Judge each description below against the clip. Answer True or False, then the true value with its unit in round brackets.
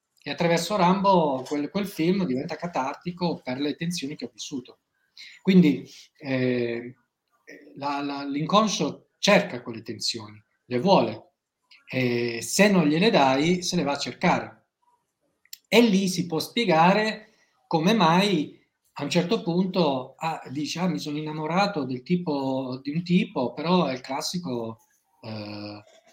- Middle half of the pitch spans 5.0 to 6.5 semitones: True (5.5 semitones)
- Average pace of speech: True (140 wpm)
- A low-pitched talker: False (155 Hz)